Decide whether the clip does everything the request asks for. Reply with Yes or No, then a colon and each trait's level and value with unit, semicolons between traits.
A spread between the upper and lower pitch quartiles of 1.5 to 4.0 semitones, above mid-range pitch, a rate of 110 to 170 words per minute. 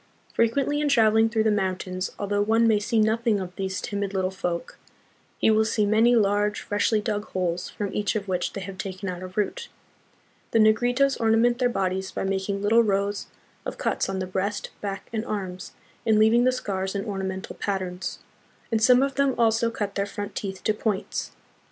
No: average, 2.7 semitones; high, 205 Hz; average, 195 wpm